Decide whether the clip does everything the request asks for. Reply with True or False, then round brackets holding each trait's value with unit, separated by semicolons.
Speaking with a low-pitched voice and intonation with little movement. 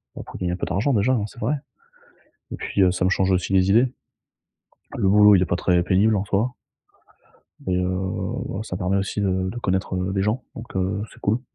True (95 Hz; 2.1 semitones)